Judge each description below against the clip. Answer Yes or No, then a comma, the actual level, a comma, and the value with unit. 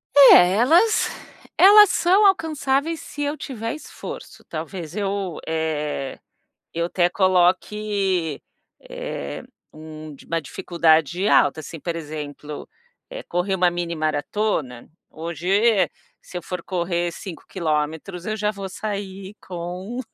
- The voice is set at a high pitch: No, medium, 180 Hz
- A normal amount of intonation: Yes, average, 4.7 semitones